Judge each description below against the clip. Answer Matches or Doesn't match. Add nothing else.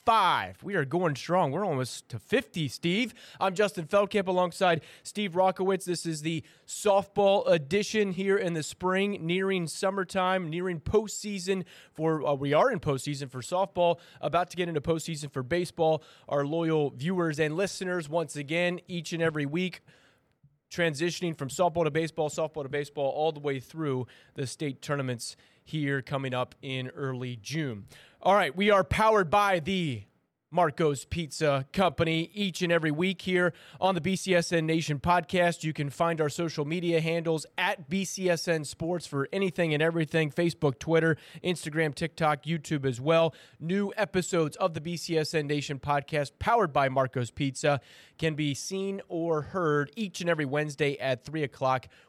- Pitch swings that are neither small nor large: Matches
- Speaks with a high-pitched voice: Doesn't match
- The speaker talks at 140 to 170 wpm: Matches